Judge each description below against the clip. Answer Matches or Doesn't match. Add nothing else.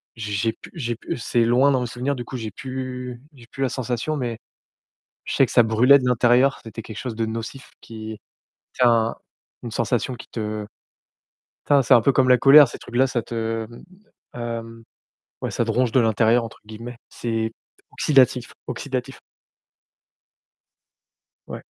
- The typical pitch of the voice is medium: Doesn't match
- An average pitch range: Doesn't match